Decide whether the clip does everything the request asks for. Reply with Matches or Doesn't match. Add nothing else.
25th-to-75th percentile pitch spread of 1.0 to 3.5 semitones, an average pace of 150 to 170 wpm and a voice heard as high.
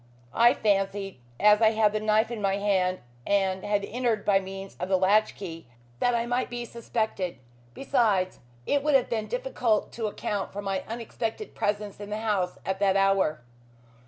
Doesn't match